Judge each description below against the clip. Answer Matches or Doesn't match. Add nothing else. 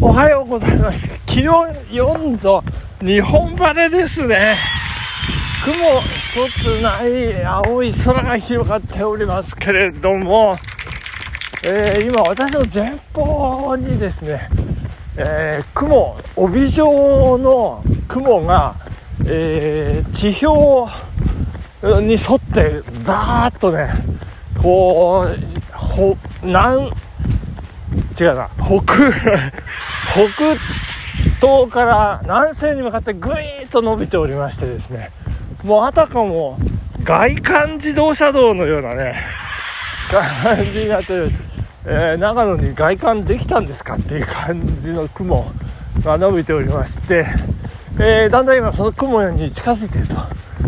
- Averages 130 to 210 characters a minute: Matches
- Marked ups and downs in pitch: Matches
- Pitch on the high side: Matches